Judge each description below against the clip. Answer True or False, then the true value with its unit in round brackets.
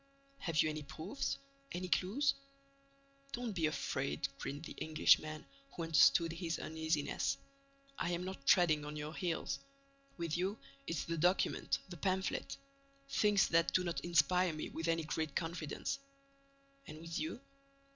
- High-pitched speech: False (165 Hz)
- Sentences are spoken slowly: False (145 wpm)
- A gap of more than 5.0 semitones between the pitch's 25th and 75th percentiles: False (2.7 semitones)